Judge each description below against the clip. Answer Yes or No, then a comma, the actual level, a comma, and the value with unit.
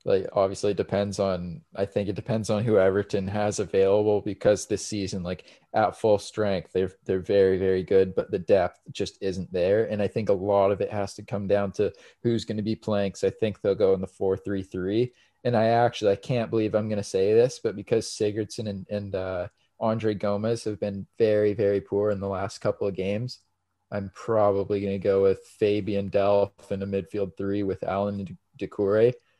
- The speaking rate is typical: No, fast, 215 wpm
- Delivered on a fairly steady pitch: Yes, narrow, 1.9 semitones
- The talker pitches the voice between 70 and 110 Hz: Yes, low, 100 Hz